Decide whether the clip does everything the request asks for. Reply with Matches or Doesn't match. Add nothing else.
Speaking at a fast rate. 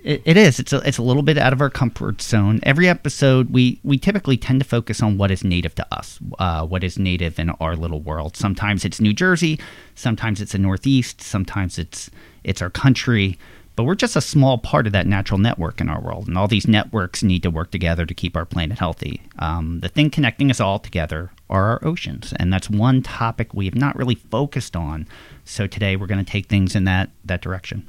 Matches